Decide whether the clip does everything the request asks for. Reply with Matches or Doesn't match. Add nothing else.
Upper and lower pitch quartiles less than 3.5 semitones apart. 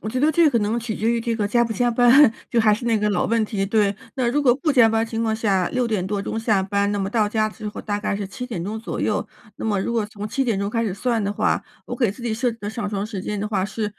Matches